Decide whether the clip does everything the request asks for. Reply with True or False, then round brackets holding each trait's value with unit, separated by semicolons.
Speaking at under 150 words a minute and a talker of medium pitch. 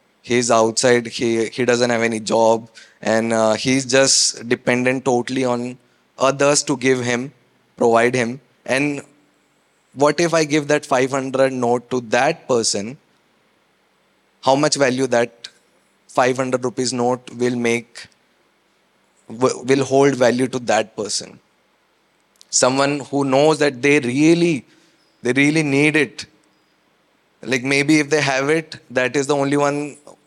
False (135 wpm; 130 Hz)